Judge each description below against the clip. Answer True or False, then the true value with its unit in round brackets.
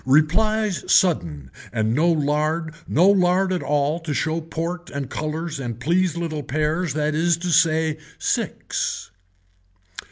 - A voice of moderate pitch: True (160 Hz)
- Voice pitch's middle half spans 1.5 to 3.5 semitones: True (2.6 semitones)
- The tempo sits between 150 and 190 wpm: False (135 wpm)